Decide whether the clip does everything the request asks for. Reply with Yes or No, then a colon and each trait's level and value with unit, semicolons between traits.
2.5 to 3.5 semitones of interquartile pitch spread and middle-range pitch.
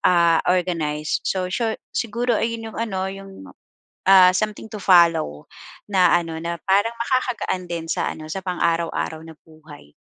No: average, 4.1 semitones; medium, 180 Hz